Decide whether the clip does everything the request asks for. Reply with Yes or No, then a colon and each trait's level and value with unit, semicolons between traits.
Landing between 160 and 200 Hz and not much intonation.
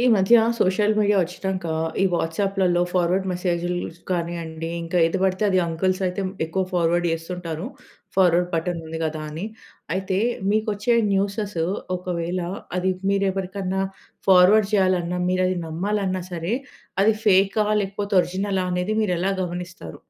Yes: medium, 185 Hz; narrow, 2.1 semitones